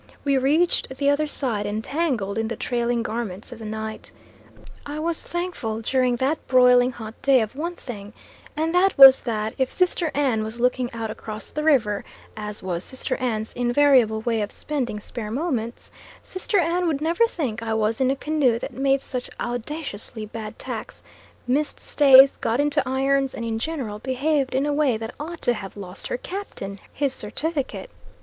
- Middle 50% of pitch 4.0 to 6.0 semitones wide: Yes, average, 4.7 semitones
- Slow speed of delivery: No, average, 180 wpm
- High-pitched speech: Yes, very high, 255 Hz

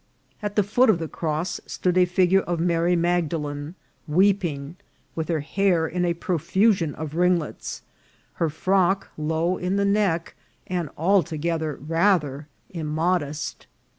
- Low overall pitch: No, medium, 170 Hz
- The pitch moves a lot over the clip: No, average, 2.8 semitones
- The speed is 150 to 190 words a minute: No, slow, 135 wpm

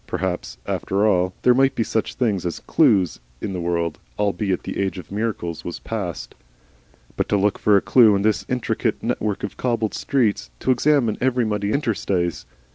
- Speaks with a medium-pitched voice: No, low, 105 Hz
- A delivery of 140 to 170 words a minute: No, average, 180 wpm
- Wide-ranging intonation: No, average, 3.9 semitones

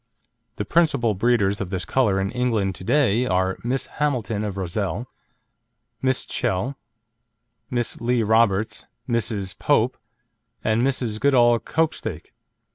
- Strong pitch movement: No, average, 4.3 semitones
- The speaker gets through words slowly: Yes, slow, 120 wpm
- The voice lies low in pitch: Yes, low, 115 Hz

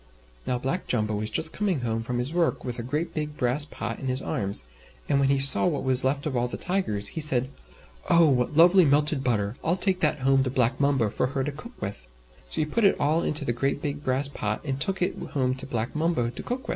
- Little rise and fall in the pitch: No, average, 3.8 semitones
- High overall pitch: No, low, 135 Hz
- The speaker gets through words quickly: Yes, fast, 250 wpm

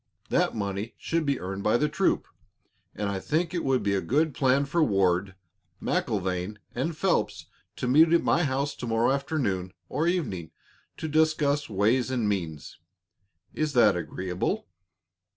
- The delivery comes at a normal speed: Yes, average, 155 wpm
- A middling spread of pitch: No, wide, 7.5 semitones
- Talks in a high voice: No, low, 125 Hz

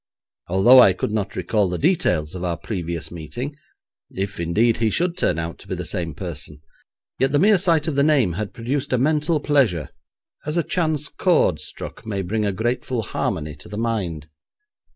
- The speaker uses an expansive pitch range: Yes, wide, 8.2 semitones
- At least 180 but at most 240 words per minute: Yes, average, 190 wpm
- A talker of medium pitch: No, low, 110 Hz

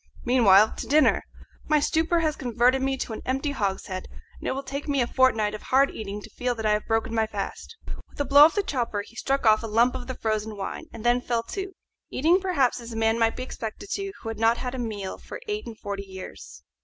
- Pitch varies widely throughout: No, average, 4.1 semitones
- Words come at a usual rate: No, fast, 250 wpm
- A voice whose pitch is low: No, high, 240 Hz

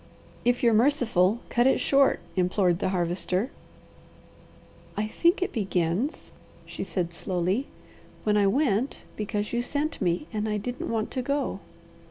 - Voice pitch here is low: No, high, 215 Hz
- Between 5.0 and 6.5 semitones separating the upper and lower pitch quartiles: Yes, average, 5.3 semitones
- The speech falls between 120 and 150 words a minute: Yes, average, 145 wpm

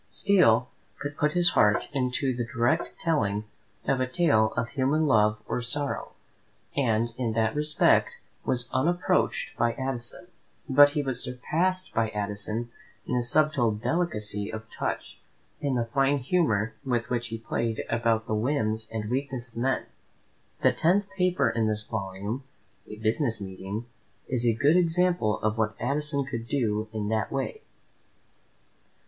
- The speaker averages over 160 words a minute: No, average, 150 wpm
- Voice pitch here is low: Yes, low, 120 Hz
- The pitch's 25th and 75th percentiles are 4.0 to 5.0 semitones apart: Yes, average, 4.7 semitones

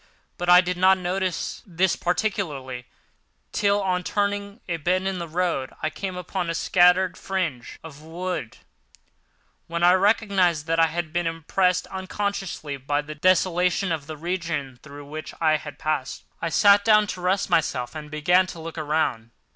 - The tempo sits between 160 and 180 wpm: Yes, average, 165 wpm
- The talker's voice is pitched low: No, medium, 175 Hz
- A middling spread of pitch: Yes, average, 3.3 semitones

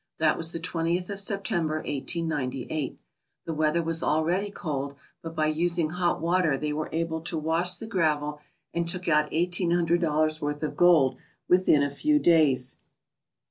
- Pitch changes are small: Yes, narrow, 2.3 semitones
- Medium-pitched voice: Yes, medium, 165 Hz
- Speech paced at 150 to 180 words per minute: Yes, average, 165 wpm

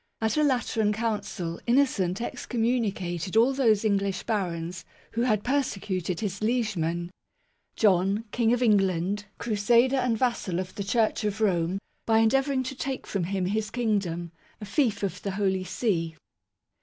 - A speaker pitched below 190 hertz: No, high, 210 Hz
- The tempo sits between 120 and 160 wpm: Yes, average, 145 wpm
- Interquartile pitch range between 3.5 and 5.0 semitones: Yes, average, 4.0 semitones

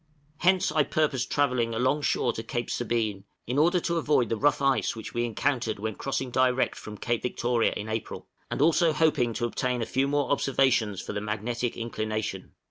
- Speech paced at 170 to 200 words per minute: Yes, average, 185 wpm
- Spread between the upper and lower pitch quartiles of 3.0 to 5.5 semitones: Yes, average, 3.9 semitones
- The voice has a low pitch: Yes, low, 120 Hz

